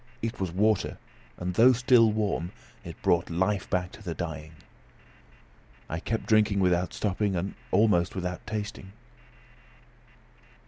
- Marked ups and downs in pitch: No, average, 3.3 semitones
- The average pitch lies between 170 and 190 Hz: No, very low, 95 Hz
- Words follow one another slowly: Yes, slow, 130 wpm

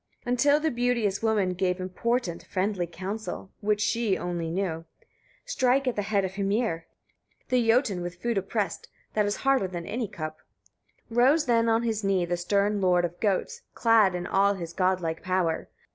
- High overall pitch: Yes, high, 200 Hz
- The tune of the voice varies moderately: Yes, average, 4.3 semitones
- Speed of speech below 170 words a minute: No, average, 175 wpm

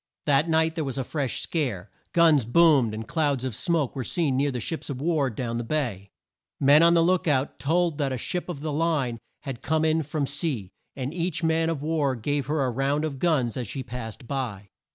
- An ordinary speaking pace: No, fast, 220 wpm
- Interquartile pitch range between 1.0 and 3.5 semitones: No, average, 4.1 semitones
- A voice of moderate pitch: Yes, medium, 145 Hz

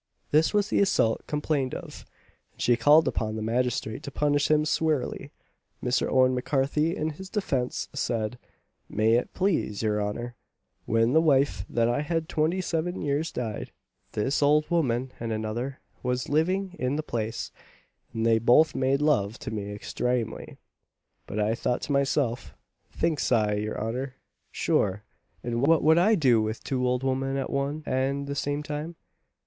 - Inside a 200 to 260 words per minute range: No, average, 165 wpm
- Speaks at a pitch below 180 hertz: Yes, low, 135 Hz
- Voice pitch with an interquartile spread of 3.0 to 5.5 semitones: Yes, average, 4.7 semitones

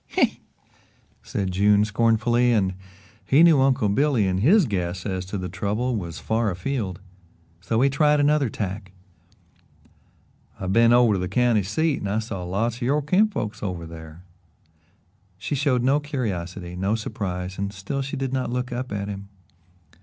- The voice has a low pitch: Yes, low, 105 Hz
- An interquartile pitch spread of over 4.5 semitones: Yes, average, 5.3 semitones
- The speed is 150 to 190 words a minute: Yes, average, 170 wpm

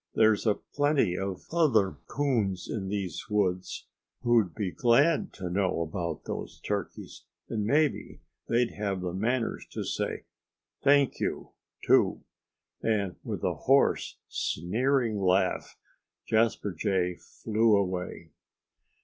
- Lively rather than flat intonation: No, average, 4.2 semitones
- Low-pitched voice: Yes, low, 105 Hz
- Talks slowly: Yes, slow, 120 wpm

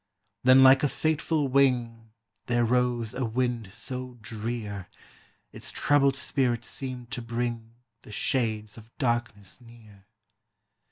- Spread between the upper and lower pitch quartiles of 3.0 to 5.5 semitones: No, narrow, 2.4 semitones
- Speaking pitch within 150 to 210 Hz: No, low, 120 Hz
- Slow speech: Yes, slow, 120 wpm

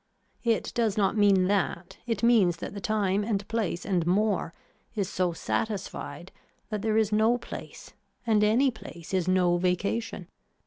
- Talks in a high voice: Yes, high, 205 Hz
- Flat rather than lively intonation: No, average, 3.1 semitones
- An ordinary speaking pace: Yes, average, 160 wpm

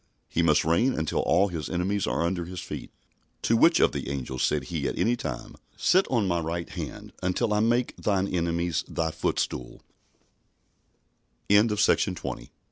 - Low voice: Yes, very low, 85 Hz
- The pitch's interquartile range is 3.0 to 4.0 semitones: No, average, 4.4 semitones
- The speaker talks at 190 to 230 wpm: No, average, 155 wpm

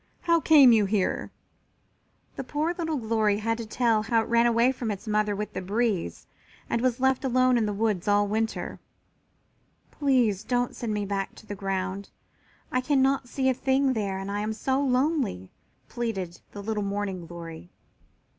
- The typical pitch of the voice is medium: No, high, 225 Hz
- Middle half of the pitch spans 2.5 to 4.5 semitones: Yes, average, 4.0 semitones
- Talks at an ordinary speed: Yes, average, 175 wpm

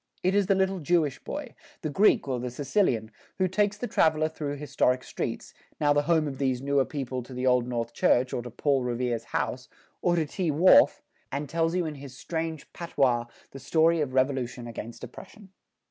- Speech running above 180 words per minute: Yes, average, 195 wpm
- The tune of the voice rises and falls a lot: No, average, 4.7 semitones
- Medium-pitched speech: Yes, medium, 145 Hz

